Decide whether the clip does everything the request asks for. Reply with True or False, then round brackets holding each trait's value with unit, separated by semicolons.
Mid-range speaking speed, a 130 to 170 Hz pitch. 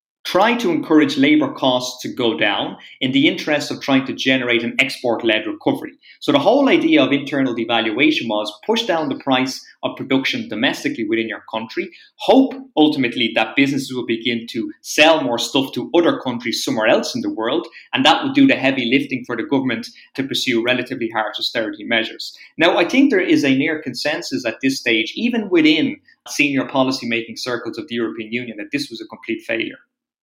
True (195 wpm; 140 Hz)